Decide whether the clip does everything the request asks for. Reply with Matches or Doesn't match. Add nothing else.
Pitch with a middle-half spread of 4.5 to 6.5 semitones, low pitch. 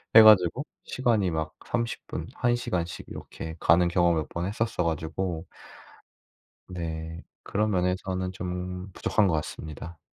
Doesn't match